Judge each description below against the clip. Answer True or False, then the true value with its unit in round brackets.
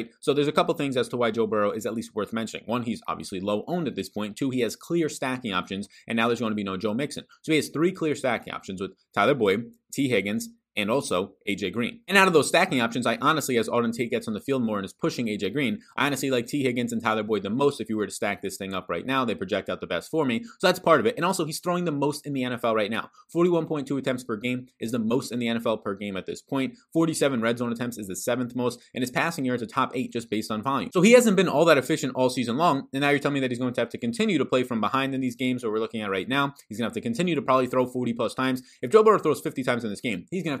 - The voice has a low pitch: True (130 Hz)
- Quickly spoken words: True (310 wpm)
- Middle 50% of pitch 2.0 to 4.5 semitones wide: False (5.5 semitones)